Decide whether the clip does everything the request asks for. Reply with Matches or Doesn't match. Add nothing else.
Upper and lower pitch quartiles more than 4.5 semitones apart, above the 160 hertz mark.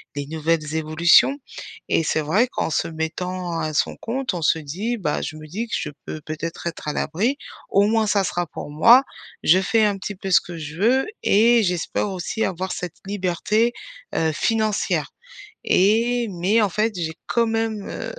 Matches